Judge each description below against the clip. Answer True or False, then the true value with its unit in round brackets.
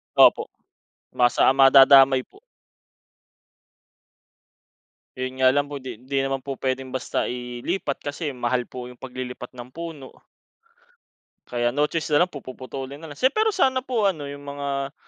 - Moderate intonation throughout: False (2.3 semitones)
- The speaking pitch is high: False (135 Hz)